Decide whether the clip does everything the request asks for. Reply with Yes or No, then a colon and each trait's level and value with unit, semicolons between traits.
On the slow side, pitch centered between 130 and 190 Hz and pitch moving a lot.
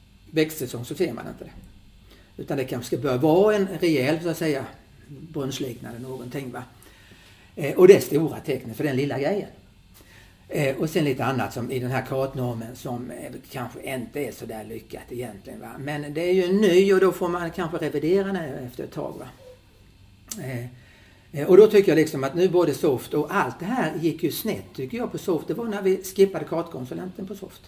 No: average, 190 wpm; low, 135 Hz; wide, 6.8 semitones